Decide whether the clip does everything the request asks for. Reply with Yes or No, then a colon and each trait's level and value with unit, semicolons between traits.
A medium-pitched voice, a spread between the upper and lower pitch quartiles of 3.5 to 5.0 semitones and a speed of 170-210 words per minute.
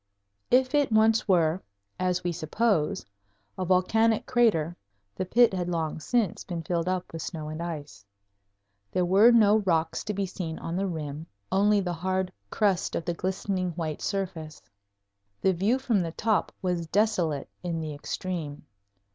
No: medium, 180 Hz; average, 3.8 semitones; average, 160 wpm